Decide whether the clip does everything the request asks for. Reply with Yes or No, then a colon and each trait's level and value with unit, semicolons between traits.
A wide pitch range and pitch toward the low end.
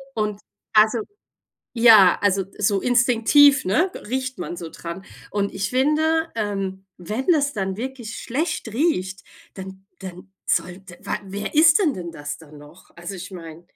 No: wide, 5.7 semitones; high, 205 Hz